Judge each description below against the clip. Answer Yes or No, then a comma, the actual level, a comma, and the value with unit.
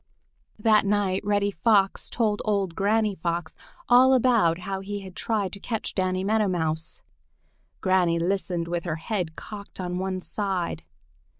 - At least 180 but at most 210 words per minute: No, average, 145 wpm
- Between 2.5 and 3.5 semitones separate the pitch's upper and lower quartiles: Yes, average, 2.9 semitones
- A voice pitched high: Yes, high, 195 Hz